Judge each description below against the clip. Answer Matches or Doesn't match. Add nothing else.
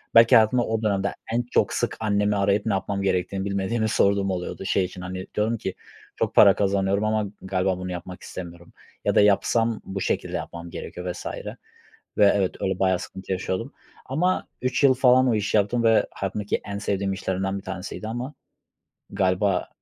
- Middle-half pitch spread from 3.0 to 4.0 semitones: Doesn't match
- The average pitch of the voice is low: Matches